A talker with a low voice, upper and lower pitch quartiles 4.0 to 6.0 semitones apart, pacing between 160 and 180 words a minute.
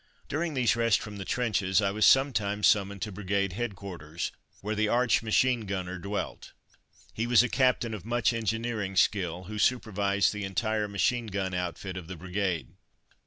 No: low, 105 Hz; average, 3.3 semitones; average, 165 wpm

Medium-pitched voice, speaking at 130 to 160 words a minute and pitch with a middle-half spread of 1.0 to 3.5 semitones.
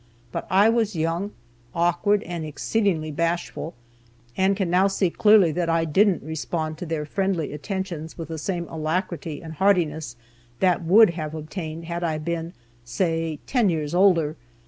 Yes: medium, 170 Hz; average, 155 wpm; average, 3.1 semitones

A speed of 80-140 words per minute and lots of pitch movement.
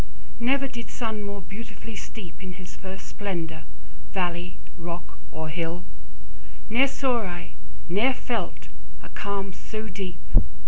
No: slow, 135 wpm; average, 4.2 semitones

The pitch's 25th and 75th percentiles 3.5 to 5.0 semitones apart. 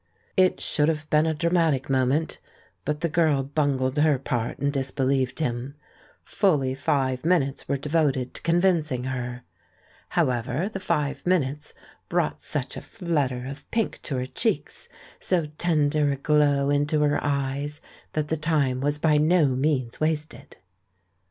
No: average, 2.9 semitones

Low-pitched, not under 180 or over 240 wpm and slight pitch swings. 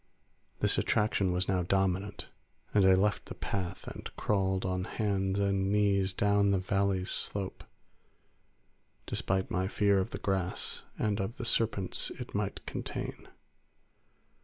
No: very low, 95 Hz; slow, 135 wpm; narrow, 1.3 semitones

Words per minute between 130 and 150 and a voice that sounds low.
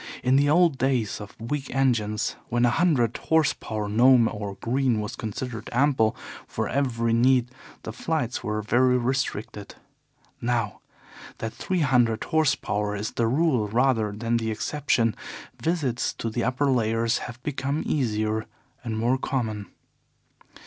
Yes: average, 145 wpm; low, 120 Hz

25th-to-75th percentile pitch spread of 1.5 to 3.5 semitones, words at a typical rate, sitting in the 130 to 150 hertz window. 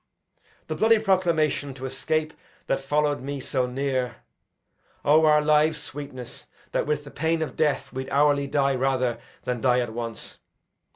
Yes: average, 2.8 semitones; average, 155 wpm; medium, 140 Hz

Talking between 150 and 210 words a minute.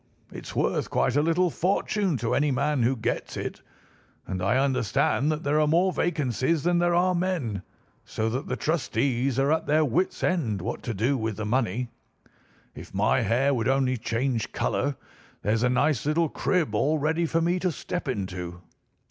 Yes: average, 180 wpm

